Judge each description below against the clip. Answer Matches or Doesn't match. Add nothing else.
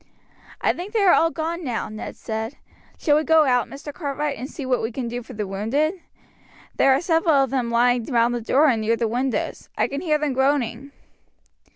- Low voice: Doesn't match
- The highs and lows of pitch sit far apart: Doesn't match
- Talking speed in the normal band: Doesn't match